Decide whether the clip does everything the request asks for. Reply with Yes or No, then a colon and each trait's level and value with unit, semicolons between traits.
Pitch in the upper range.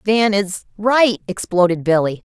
Yes: high, 200 Hz